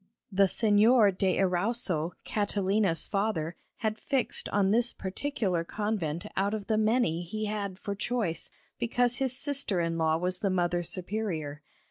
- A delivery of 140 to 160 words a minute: Yes, average, 145 wpm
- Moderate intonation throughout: Yes, average, 3.8 semitones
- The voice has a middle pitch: No, high, 200 Hz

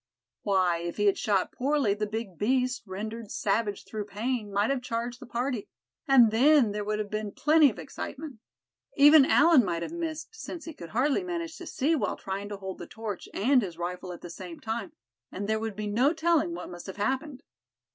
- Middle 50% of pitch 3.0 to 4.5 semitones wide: No, wide, 5.4 semitones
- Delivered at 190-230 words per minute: Yes, fast, 205 wpm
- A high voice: Yes, high, 220 Hz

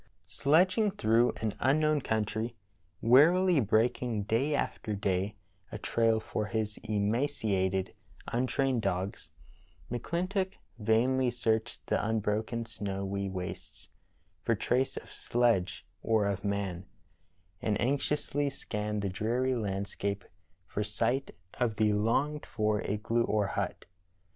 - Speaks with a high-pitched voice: No, low, 110 Hz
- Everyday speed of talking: No, slow, 120 wpm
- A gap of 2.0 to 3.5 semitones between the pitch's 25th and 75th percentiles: No, average, 3.9 semitones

